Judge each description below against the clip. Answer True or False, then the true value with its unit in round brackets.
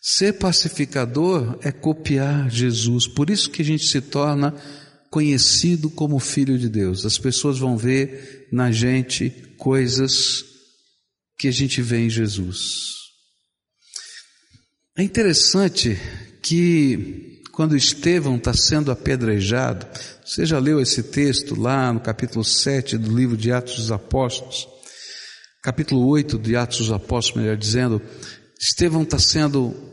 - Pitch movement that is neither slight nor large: True (3.3 semitones)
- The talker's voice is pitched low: True (130 Hz)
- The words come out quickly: False (130 wpm)